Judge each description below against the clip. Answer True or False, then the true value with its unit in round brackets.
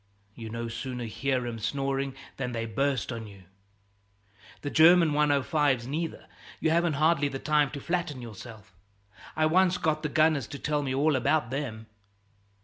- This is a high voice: False (140 Hz)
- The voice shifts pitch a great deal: False (4.3 semitones)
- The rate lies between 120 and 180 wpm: True (160 wpm)